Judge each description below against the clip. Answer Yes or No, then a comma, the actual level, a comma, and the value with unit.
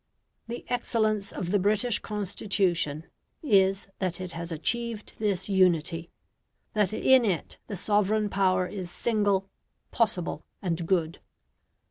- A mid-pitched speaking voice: No, high, 195 Hz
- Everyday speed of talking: No, slow, 120 wpm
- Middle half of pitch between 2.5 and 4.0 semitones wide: Yes, average, 3.2 semitones